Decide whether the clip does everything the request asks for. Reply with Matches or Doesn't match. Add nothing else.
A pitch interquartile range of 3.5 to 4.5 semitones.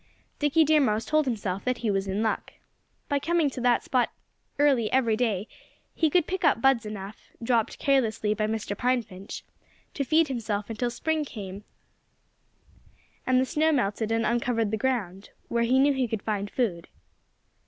Matches